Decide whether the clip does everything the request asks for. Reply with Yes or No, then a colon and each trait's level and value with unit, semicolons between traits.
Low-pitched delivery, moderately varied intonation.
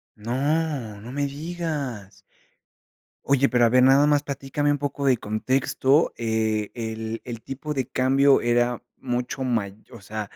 Yes: low, 130 Hz; average, 3.9 semitones